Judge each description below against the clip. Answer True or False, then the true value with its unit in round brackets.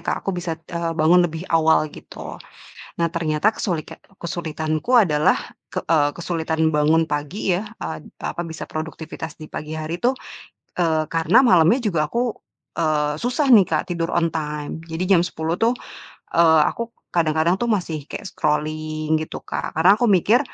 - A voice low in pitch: False (165 Hz)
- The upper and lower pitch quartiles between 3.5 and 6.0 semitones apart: False (2.7 semitones)